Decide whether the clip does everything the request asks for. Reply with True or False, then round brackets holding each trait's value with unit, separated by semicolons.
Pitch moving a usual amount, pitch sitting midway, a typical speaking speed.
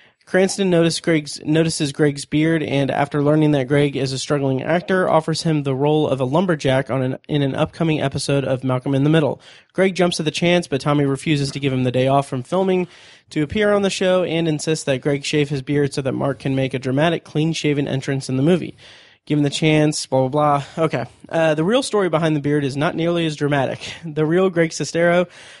False (3.0 semitones; 150 Hz; 225 wpm)